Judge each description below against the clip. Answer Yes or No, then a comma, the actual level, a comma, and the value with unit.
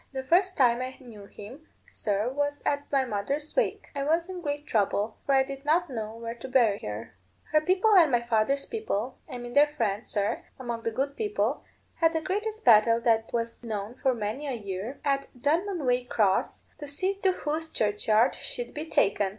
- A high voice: Yes, very high, 265 Hz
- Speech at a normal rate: Yes, average, 190 wpm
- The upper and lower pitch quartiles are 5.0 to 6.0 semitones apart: Yes, average, 5.3 semitones